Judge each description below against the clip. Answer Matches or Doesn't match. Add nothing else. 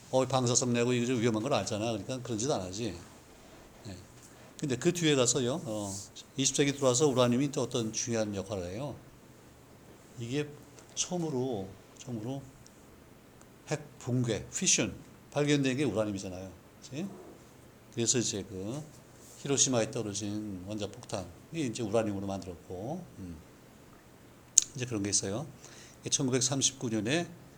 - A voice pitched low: Matches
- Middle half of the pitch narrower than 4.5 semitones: Matches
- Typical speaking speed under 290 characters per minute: Matches